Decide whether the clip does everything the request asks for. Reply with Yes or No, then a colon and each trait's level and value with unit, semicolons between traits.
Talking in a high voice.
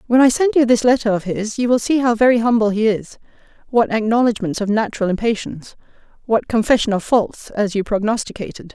Yes: high, 225 Hz